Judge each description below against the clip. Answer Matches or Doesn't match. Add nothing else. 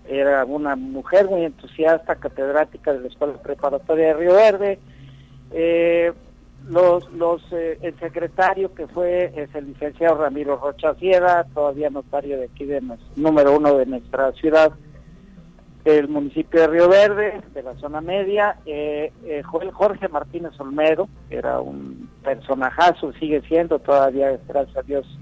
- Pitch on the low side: Doesn't match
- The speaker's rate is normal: Matches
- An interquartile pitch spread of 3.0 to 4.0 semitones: Matches